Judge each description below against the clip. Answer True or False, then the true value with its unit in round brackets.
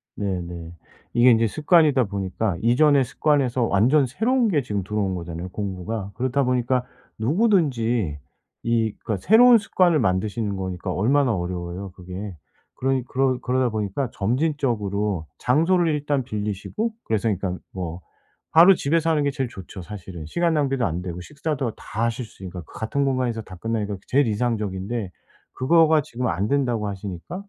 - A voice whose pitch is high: False (115 Hz)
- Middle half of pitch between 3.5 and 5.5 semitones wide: False (6.4 semitones)